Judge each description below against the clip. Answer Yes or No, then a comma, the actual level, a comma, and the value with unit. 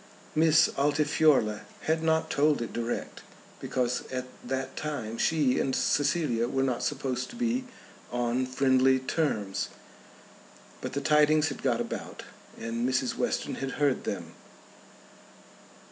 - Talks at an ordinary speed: No, slow, 130 wpm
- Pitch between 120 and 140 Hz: Yes, low, 135 Hz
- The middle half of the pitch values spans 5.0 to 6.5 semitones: No, average, 3.4 semitones